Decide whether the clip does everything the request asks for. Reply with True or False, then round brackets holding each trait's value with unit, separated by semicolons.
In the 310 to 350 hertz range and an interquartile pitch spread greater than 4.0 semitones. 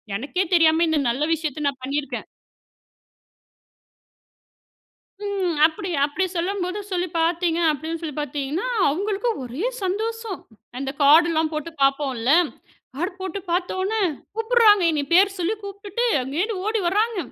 True (345 Hz; 5.2 semitones)